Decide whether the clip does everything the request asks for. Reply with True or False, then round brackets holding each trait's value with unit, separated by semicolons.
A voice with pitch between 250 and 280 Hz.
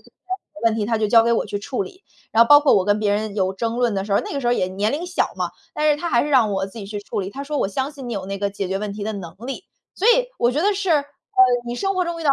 False (230 Hz)